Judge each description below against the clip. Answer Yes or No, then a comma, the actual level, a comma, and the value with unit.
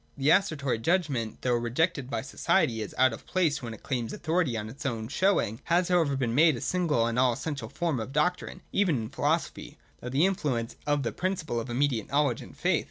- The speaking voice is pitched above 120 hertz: Yes, medium, 140 Hz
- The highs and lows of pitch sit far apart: Yes, wide, 5.8 semitones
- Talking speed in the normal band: No, fast, 220 wpm